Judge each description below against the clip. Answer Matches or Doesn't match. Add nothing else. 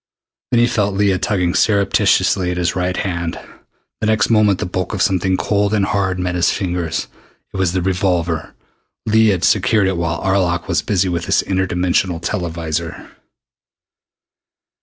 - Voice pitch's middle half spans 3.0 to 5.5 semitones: Doesn't match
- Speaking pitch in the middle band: Doesn't match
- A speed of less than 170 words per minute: Matches